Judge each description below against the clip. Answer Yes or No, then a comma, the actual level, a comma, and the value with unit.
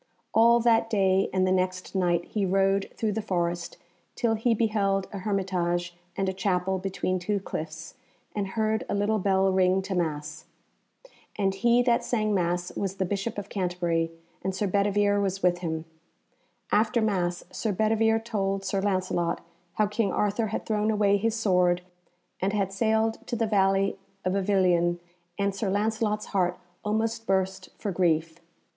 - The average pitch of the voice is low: No, high, 195 Hz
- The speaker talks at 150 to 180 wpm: Yes, average, 165 wpm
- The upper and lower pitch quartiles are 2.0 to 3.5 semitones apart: Yes, narrow, 2.6 semitones